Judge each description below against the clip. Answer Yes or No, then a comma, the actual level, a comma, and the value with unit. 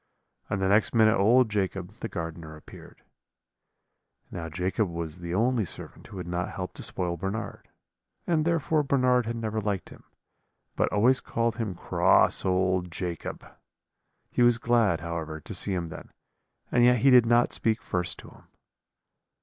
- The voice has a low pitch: Yes, low, 100 Hz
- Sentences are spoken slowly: No, average, 165 wpm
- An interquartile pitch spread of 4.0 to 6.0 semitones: Yes, average, 5.0 semitones